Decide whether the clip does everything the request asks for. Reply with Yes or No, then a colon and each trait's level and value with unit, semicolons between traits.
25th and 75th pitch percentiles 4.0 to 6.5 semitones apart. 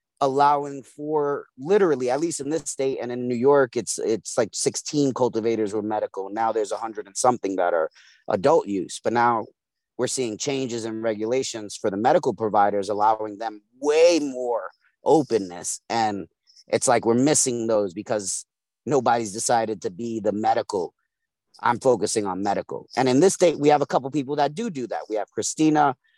Yes: average, 4.8 semitones